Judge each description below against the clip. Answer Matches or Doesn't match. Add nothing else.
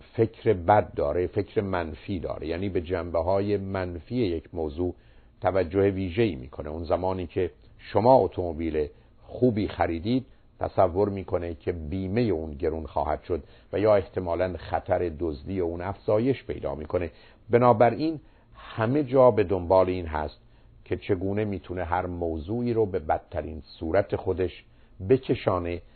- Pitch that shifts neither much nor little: Matches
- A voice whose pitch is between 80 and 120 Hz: Matches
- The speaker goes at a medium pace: Matches